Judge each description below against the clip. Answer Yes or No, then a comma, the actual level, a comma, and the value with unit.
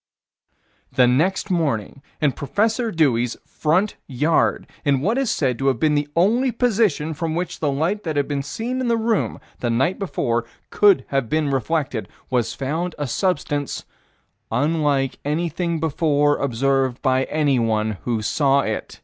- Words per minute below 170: Yes, average, 155 wpm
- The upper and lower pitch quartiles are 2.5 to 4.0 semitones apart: No, average, 4.7 semitones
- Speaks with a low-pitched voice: No, medium, 145 Hz